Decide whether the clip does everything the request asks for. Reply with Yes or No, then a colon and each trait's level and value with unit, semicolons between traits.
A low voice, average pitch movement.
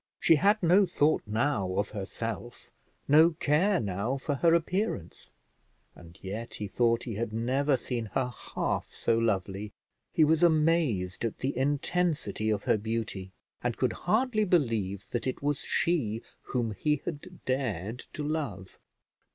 No: low, 125 Hz; wide, 6.7 semitones